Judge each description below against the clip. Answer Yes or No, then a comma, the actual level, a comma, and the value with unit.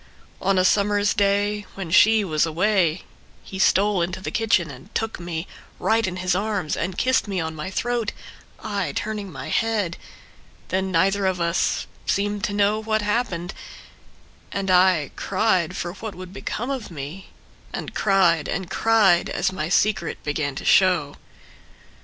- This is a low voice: No, high, 190 Hz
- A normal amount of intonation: Yes, average, 3.2 semitones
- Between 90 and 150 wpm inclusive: No, average, 160 wpm